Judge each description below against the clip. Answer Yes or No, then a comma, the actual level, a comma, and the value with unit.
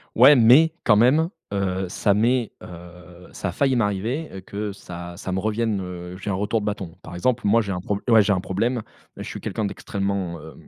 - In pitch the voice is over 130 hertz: No, low, 100 Hz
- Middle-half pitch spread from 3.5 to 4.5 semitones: Yes, average, 4.1 semitones